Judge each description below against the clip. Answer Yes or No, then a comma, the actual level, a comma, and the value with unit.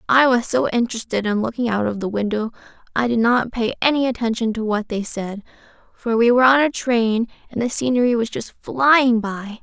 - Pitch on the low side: No, high, 230 Hz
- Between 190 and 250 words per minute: Yes, fast, 205 wpm